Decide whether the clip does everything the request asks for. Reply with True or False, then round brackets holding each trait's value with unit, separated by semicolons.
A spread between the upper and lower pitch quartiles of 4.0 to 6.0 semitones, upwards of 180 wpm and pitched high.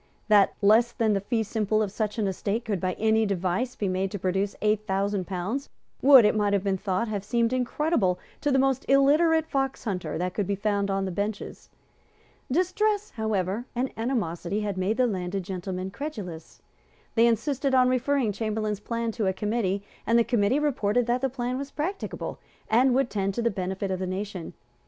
True (4.3 semitones; 190 wpm; 215 Hz)